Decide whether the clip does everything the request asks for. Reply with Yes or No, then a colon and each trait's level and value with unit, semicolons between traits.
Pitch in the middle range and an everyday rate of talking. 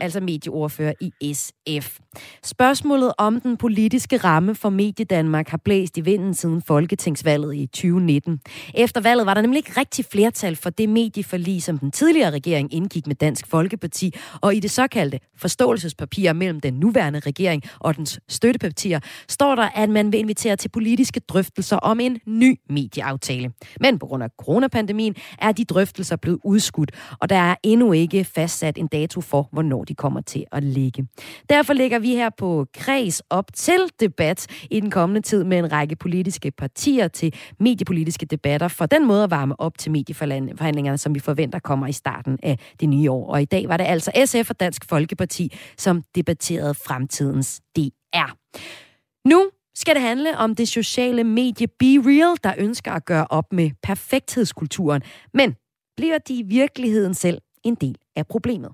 Yes: medium, 180 Hz; average, 170 wpm